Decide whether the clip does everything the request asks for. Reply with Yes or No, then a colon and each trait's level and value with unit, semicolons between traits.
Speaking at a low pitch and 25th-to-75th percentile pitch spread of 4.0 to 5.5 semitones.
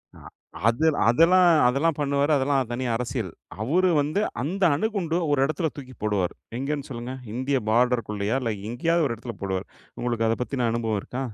Yes: low, 130 Hz; average, 4.3 semitones